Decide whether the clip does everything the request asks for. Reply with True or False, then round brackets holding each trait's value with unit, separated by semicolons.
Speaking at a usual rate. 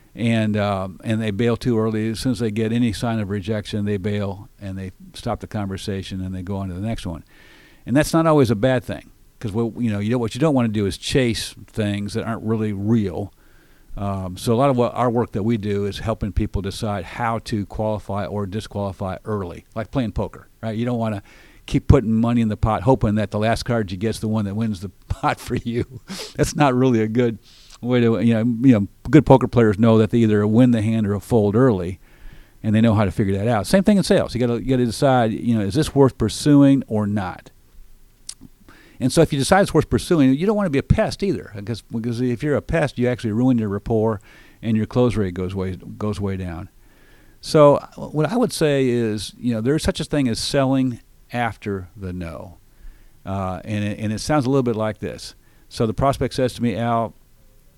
False (235 wpm)